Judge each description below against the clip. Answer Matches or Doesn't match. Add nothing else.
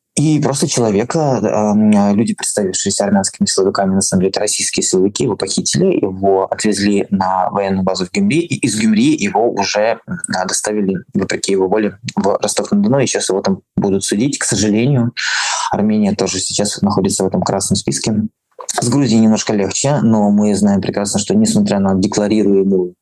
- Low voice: Matches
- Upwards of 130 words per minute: Matches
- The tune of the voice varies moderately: Doesn't match